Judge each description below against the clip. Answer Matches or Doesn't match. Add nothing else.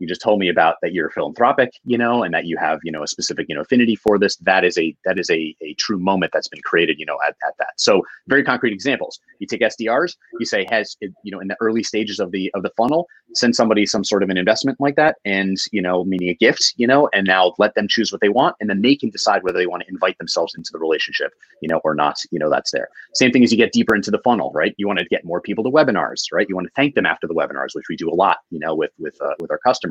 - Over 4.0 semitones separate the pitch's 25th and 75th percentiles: Matches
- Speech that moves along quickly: Matches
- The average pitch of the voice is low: Matches